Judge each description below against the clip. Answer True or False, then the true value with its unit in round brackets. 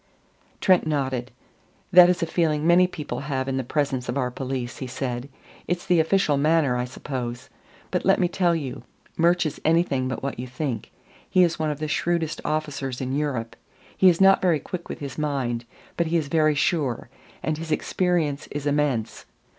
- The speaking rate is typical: True (190 wpm)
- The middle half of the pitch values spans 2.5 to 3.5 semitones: False (4.1 semitones)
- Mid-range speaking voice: True (150 Hz)